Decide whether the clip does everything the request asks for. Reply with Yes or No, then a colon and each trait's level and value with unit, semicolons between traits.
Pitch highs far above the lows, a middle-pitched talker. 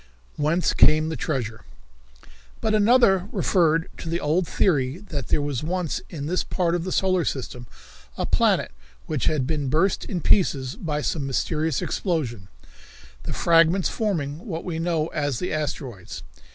No: average, 3.8 semitones; medium, 160 Hz